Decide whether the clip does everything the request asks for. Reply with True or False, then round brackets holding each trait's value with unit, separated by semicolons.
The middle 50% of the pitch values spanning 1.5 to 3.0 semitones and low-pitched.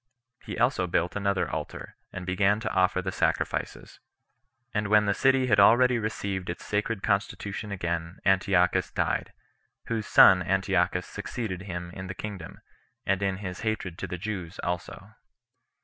True (2.5 semitones; 95 Hz)